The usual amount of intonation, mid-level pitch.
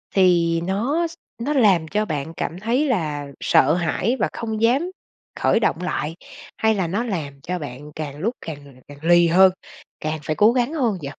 No: wide, 6.5 semitones; medium, 180 Hz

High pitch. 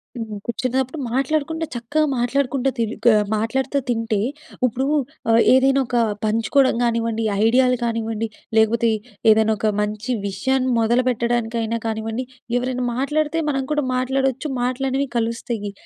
Yes: high, 245 Hz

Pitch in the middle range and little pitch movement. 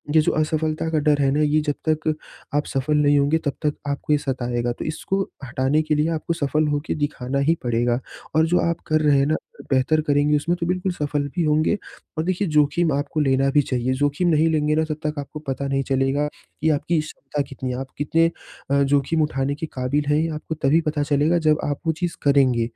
Yes: medium, 150 Hz; narrow, 2.1 semitones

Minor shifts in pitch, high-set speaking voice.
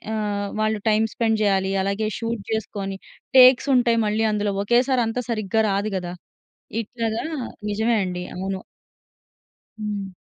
Yes: narrow, 2.3 semitones; high, 215 Hz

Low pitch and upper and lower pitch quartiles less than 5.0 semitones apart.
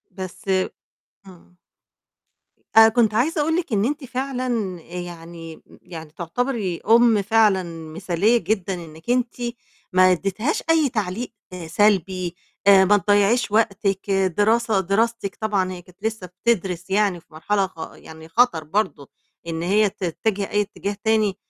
No: high, 200 Hz; average, 3.8 semitones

